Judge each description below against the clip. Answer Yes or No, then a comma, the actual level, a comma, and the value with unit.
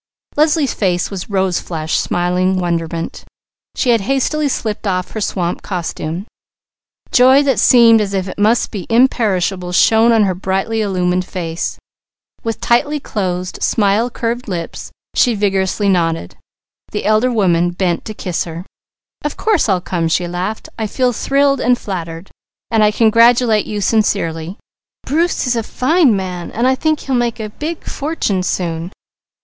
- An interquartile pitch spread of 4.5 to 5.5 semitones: Yes, average, 4.9 semitones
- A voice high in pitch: Yes, high, 205 Hz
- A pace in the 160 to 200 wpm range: No, average, 150 wpm